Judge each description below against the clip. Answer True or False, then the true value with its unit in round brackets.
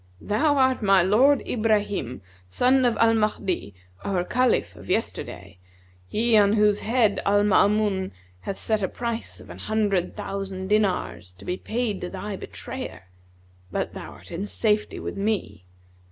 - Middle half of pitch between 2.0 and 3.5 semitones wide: True (2.9 semitones)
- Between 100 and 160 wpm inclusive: True (155 wpm)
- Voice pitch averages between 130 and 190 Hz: False (205 Hz)